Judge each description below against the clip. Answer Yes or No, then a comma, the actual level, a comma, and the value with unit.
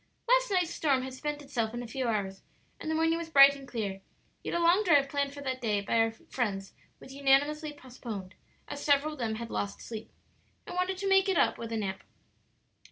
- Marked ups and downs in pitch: Yes, wide, 5.7 semitones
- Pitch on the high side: Yes, very high, 275 Hz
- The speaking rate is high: Yes, fast, 220 wpm